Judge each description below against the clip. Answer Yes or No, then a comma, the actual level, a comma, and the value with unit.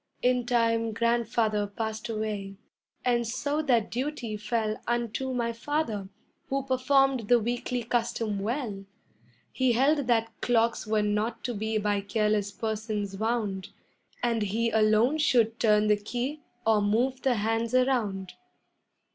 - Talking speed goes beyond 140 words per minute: No, slow, 135 wpm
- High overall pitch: Yes, high, 230 Hz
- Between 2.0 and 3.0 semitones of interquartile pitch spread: Yes, narrow, 2.5 semitones